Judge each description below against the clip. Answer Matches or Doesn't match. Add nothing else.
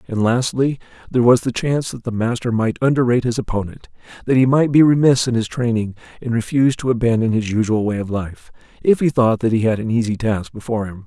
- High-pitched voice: Doesn't match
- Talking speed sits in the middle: Doesn't match